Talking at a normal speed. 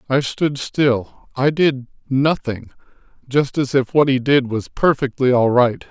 Yes: average, 165 wpm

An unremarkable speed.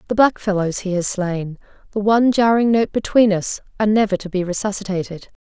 Yes: average, 165 wpm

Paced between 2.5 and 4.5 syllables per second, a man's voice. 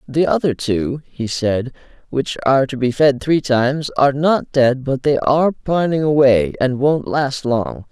Yes: 4.3 syllables/s; male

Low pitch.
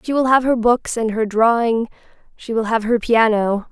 No: high, 230 Hz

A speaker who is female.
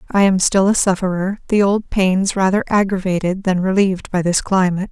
Yes: female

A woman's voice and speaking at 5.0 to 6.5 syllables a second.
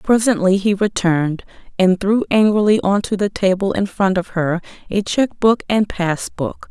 No: female; 4.7 syllables/s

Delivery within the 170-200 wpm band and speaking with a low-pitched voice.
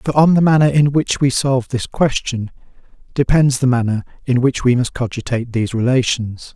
Yes: average, 185 wpm; low, 130 Hz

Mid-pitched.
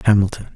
No: low, 100 Hz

